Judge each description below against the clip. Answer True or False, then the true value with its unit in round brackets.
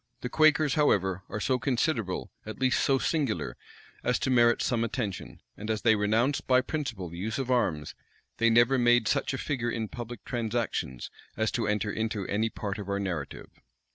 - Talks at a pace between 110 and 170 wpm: False (185 wpm)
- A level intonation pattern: False (3.5 semitones)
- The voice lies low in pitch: True (115 Hz)